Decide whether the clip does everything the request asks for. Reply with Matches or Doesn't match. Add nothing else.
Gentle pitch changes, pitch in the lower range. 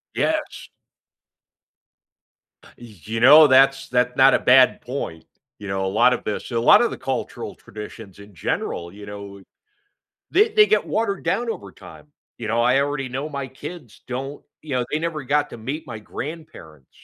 Doesn't match